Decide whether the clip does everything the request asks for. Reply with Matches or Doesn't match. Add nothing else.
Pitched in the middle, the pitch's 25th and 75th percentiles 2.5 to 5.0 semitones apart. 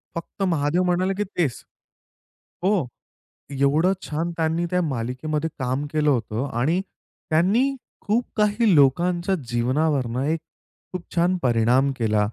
Doesn't match